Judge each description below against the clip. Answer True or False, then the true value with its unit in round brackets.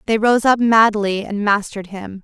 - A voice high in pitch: True (210 Hz)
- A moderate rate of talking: True (190 wpm)